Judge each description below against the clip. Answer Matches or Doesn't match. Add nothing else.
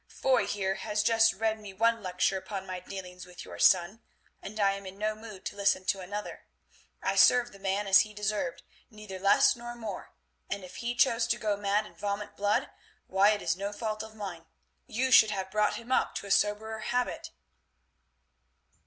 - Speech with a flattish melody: Matches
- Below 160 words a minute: Doesn't match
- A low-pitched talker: Doesn't match